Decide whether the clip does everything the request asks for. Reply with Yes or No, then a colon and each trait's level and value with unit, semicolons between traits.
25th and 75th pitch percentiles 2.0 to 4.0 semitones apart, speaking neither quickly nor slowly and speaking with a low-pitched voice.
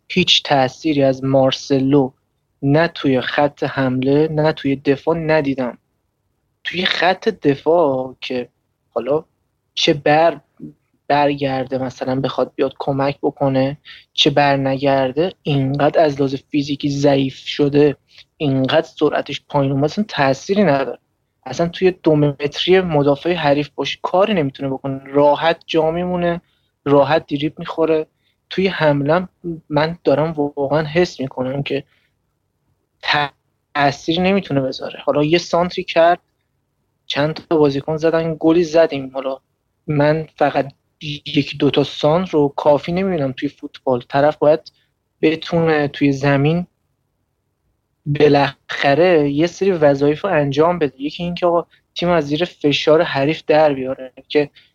No: average, 2.8 semitones; average, 125 wpm; medium, 145 Hz